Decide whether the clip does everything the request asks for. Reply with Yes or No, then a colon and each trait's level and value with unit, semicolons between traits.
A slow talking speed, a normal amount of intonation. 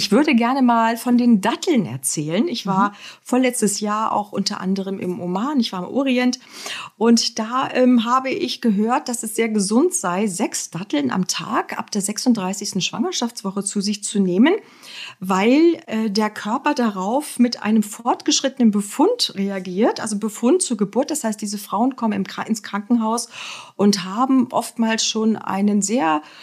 No: average, 165 wpm; average, 3.6 semitones